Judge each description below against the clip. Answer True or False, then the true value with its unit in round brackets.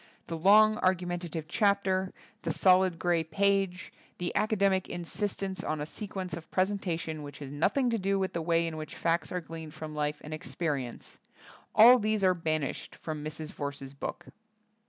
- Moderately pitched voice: True (175 Hz)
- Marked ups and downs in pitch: False (3.7 semitones)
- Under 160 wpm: False (175 wpm)